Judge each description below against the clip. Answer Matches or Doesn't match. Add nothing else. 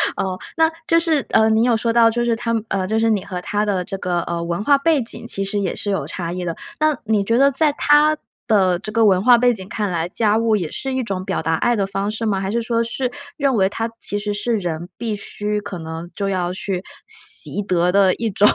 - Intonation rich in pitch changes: Doesn't match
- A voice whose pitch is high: Matches